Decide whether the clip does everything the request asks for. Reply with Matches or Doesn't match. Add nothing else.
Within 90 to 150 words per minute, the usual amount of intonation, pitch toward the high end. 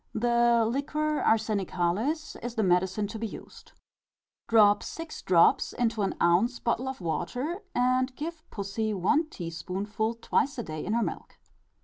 Matches